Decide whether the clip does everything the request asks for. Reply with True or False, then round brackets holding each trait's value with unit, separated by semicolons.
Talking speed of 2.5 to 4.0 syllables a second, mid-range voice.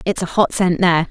False (6.1 syllables/s; 180 Hz)